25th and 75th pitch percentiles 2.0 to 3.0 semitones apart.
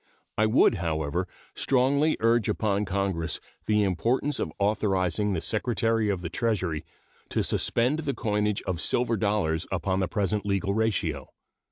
No: average, 3.6 semitones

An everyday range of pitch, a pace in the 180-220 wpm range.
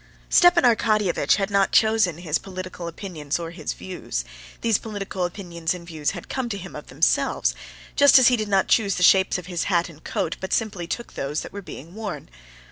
Yes: average, 4.0 semitones; fast, 205 wpm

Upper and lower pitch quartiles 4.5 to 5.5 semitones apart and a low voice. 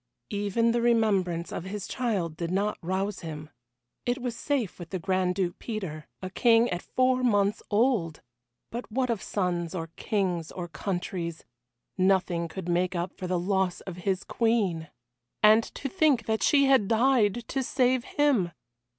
No: average, 4.9 semitones; high, 195 Hz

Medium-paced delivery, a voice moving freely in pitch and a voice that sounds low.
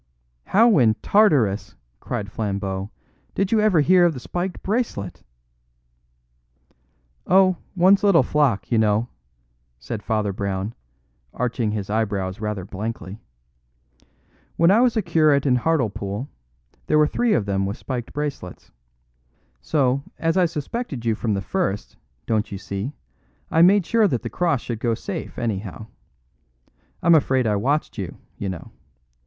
Yes: average, 145 wpm; wide, 8.6 semitones; low, 125 Hz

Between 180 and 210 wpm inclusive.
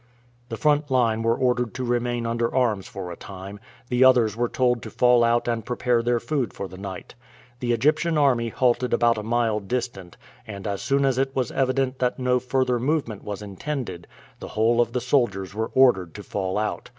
Yes: average, 200 wpm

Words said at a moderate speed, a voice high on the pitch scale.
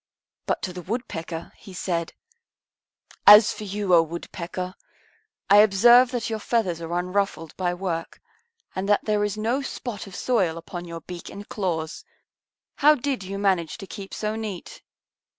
Yes: average, 160 wpm; high, 195 Hz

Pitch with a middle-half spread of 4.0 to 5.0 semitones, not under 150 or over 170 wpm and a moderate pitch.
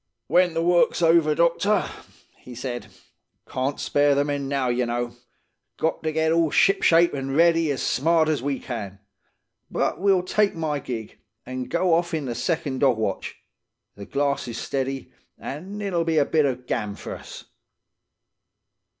Yes: average, 4.5 semitones; average, 165 wpm; medium, 145 Hz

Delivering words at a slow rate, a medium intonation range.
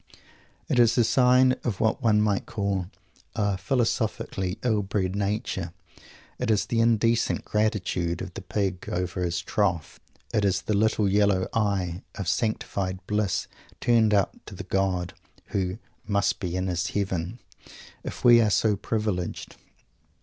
No: average, 150 wpm; average, 3.0 semitones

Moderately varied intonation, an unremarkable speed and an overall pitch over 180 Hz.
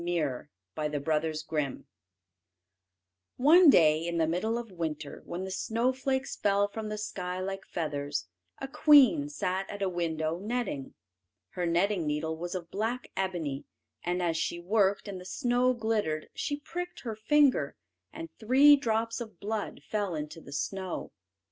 No: wide, 5.9 semitones; average, 155 wpm; high, 190 Hz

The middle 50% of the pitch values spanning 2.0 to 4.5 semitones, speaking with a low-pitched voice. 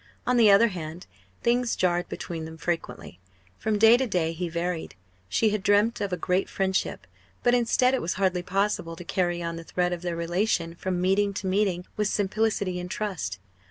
No: average, 3.4 semitones; medium, 185 Hz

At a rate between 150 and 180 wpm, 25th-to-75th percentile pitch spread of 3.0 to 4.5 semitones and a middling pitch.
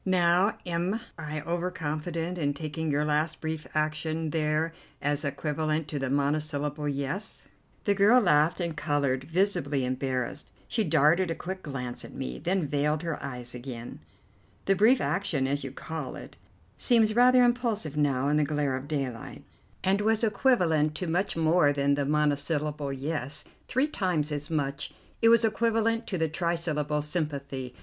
Yes: average, 160 wpm; average, 3.9 semitones; medium, 155 Hz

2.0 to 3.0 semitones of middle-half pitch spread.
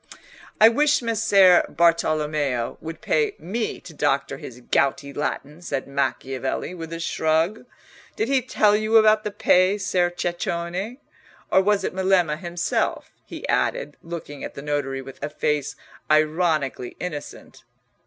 No: wide, 5.5 semitones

